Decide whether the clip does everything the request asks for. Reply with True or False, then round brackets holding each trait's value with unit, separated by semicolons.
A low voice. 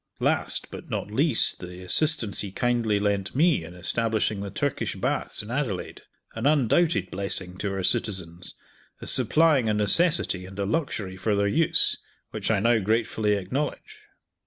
True (105 Hz)